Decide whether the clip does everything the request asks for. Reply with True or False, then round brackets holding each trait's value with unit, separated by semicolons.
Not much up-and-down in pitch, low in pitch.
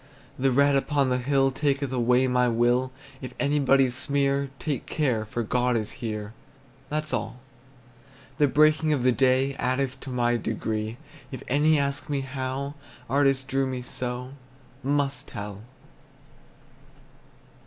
True (2.2 semitones; 130 Hz)